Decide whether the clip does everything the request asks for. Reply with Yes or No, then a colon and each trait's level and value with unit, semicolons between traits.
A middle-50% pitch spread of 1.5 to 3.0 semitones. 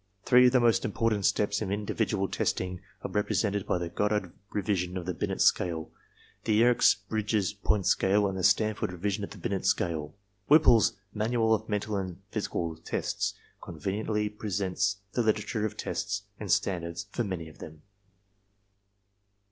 Yes: average, 2.7 semitones